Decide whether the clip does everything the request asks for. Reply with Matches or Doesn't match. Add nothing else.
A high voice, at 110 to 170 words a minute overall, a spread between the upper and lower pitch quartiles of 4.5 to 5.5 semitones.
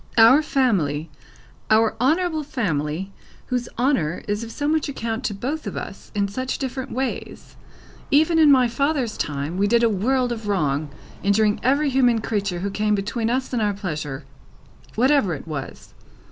Matches